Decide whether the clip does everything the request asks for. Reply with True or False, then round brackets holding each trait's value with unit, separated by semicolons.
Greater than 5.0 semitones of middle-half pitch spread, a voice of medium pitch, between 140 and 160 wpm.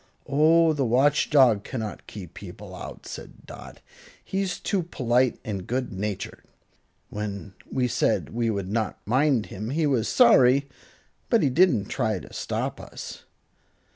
False (5.5 semitones; 125 Hz; 145 wpm)